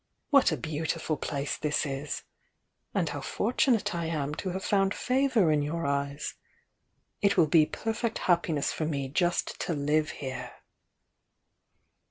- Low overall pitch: No, medium, 160 Hz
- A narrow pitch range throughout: No, average, 4.5 semitones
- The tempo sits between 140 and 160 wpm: Yes, average, 150 wpm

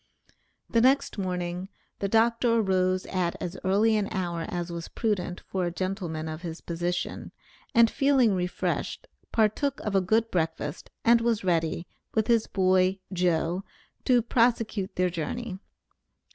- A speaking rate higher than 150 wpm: No, average, 145 wpm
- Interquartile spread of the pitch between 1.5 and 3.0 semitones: No, average, 4.3 semitones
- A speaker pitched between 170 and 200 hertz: Yes, high, 190 Hz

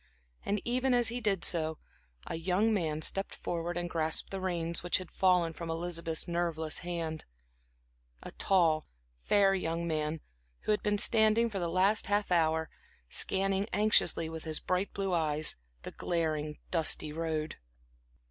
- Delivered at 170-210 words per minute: No, average, 155 wpm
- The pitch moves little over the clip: No, average, 3.4 semitones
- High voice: No, medium, 170 Hz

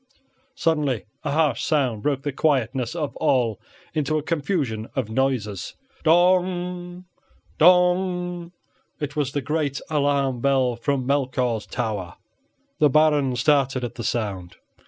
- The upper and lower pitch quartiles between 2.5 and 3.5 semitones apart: No, average, 4.3 semitones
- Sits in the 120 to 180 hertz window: Yes, medium, 140 Hz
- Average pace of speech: No, slow, 125 wpm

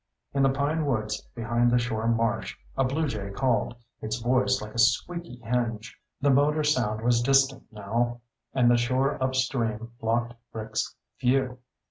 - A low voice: Yes, low, 120 Hz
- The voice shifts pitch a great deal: No, average, 2.8 semitones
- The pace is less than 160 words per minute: Yes, average, 150 wpm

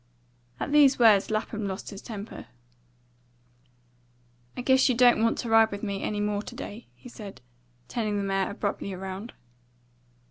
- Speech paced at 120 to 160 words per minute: Yes, average, 155 wpm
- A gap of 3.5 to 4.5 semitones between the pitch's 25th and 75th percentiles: No, average, 2.8 semitones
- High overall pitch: Yes, high, 215 Hz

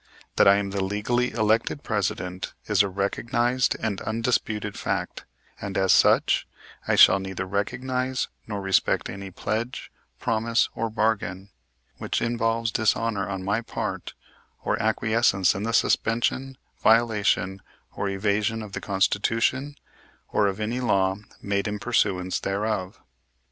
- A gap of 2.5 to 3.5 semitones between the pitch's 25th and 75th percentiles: Yes, average, 2.8 semitones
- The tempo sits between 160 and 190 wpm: No, slow, 135 wpm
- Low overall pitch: Yes, low, 105 Hz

